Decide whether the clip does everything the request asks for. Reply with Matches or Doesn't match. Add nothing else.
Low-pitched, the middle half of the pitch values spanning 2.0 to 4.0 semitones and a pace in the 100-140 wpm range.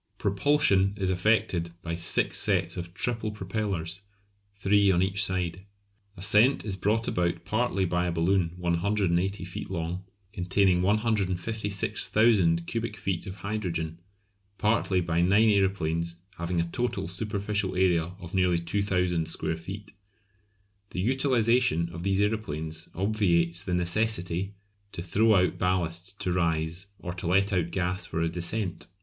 Matches